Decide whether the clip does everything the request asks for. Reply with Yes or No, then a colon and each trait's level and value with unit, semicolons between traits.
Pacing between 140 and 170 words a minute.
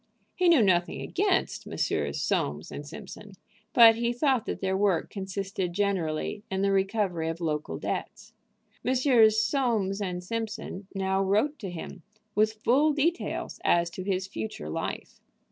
Yes: average, 145 wpm